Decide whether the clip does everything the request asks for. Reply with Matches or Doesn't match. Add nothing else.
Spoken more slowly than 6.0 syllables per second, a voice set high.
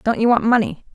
Doesn't match